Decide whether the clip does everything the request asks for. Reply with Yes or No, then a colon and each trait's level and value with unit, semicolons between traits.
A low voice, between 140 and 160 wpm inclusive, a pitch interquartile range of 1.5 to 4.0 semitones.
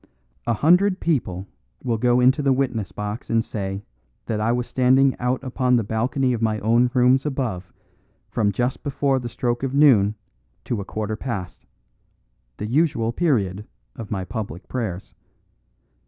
Yes: low, 120 Hz; average, 155 wpm; average, 3.7 semitones